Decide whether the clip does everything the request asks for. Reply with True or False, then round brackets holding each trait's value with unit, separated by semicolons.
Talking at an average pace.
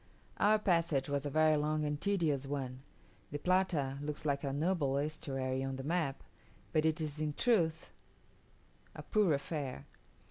True (150 wpm)